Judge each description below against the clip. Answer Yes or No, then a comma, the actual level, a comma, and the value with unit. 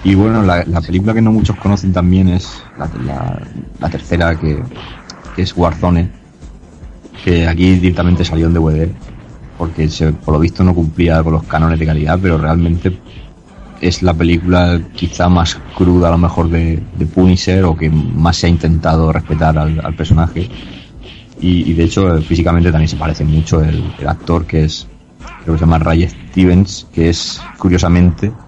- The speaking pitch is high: No, very low, 85 Hz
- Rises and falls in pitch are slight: Yes, narrow, 2.0 semitones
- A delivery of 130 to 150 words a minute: No, average, 175 wpm